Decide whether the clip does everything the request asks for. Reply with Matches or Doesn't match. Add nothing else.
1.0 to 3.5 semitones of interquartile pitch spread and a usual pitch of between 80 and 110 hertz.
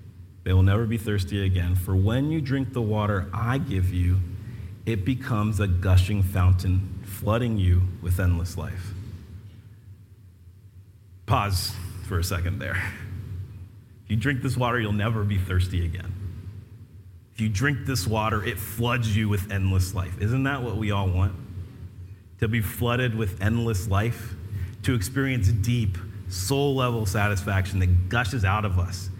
Matches